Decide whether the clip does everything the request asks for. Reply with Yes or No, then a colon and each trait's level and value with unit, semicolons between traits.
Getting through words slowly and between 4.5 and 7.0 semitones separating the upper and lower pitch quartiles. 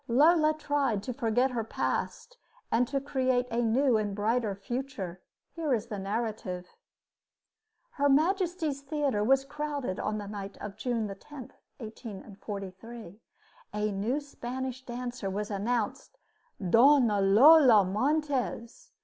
Yes: slow, 120 wpm; average, 4.9 semitones